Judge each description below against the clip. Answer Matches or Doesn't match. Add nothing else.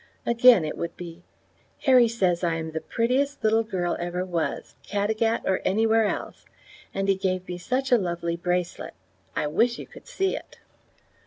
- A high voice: Matches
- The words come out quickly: Doesn't match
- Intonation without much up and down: Doesn't match